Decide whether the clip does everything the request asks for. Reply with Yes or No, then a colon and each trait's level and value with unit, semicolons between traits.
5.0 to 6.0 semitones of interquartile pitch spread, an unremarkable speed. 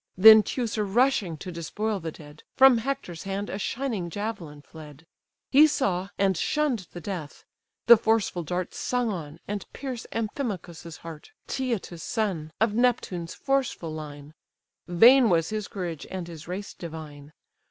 Yes: wide, 5.5 semitones; average, 145 wpm